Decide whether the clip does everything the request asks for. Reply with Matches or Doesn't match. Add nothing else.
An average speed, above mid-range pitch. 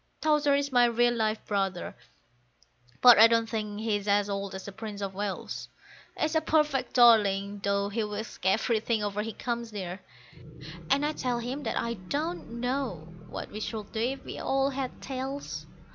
Matches